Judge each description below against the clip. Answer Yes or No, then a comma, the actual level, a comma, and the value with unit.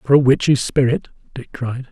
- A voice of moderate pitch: No, low, 130 Hz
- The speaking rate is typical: Yes, average, 190 wpm